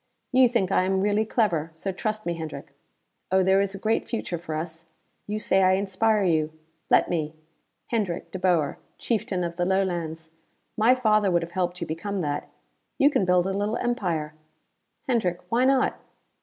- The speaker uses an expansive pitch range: No, average, 4.0 semitones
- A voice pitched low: No, high, 190 Hz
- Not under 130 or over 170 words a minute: No, average, 180 wpm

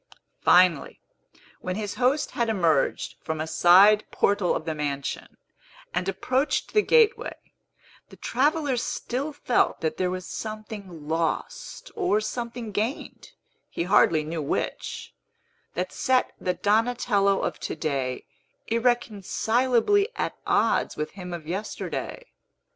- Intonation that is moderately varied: No, wide, 6.5 semitones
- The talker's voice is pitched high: Yes, high, 205 Hz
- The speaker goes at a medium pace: No, slow, 125 wpm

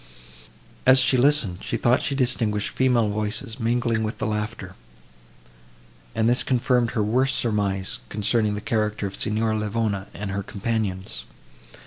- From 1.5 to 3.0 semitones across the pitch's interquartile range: Yes, average, 2.7 semitones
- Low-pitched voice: Yes, low, 110 Hz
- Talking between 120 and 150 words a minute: Yes, average, 140 wpm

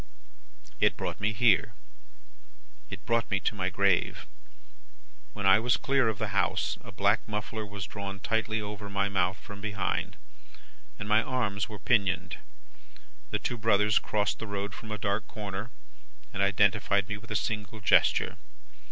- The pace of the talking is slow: No, average, 160 wpm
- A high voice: No, low, 105 Hz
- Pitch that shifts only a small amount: Yes, narrow, 1.7 semitones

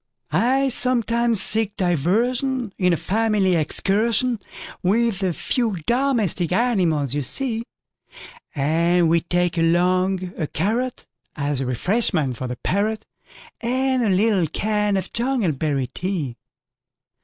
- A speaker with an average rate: No, slow, 95 wpm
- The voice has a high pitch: Yes, high, 195 Hz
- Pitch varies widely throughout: Yes, wide, 5.7 semitones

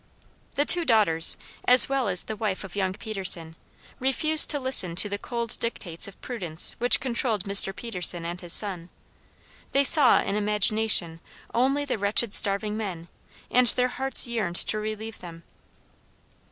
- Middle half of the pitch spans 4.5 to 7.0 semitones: Yes, average, 4.9 semitones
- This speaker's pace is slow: No, average, 155 wpm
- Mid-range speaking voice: No, high, 210 Hz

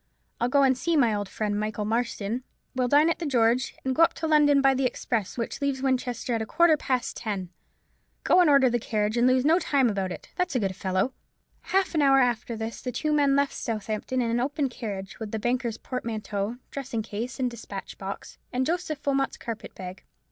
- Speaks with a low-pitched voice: No, high, 245 Hz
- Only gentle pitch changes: No, average, 4.1 semitones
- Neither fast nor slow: No, fast, 215 wpm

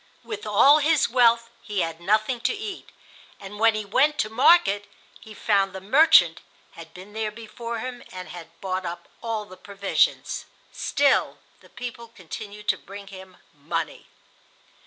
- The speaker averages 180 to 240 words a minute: No, average, 155 wpm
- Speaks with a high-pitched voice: Yes, high, 210 Hz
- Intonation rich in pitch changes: No, average, 3.9 semitones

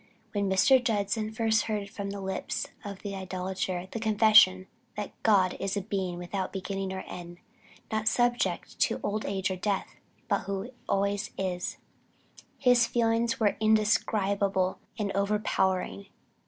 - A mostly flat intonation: Yes, narrow, 2.3 semitones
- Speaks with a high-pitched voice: Yes, high, 200 Hz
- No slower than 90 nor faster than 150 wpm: Yes, average, 140 wpm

